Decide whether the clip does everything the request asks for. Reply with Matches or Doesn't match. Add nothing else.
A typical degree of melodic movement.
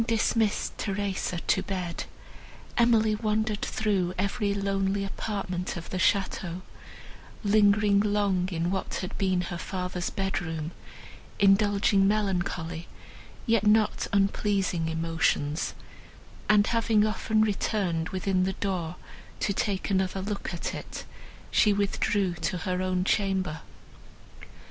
Doesn't match